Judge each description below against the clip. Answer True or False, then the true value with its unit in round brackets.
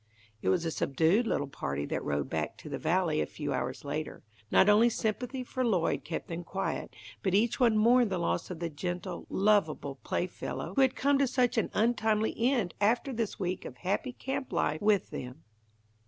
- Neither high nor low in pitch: False (195 Hz)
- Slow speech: False (195 wpm)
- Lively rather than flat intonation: True (6.5 semitones)